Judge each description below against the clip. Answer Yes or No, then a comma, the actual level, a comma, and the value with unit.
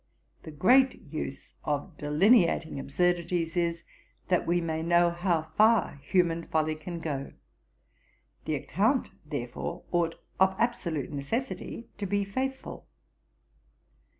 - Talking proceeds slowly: Yes, slow, 115 wpm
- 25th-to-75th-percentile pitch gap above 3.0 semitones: Yes, average, 3.8 semitones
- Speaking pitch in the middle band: Yes, medium, 170 Hz